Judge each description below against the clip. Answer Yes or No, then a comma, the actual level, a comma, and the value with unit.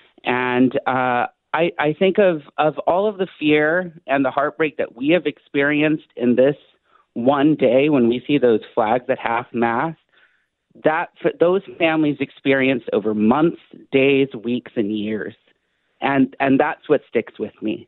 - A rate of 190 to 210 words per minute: No, average, 160 wpm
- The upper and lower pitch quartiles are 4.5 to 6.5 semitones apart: No, average, 3.7 semitones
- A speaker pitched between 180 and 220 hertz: No, medium, 140 Hz